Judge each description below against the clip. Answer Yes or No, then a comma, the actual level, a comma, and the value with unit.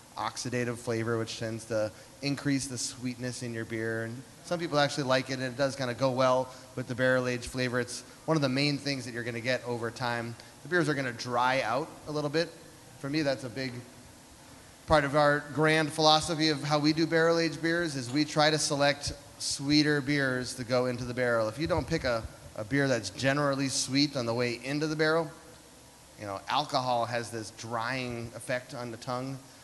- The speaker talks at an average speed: No, fast, 215 wpm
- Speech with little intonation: No, average, 3.3 semitones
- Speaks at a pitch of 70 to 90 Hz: No, low, 130 Hz